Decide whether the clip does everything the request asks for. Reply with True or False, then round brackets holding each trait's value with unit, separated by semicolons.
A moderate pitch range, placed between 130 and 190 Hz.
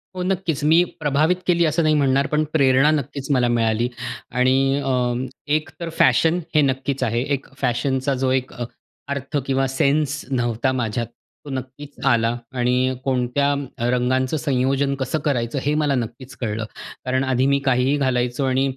False (2.3 semitones; 135 Hz)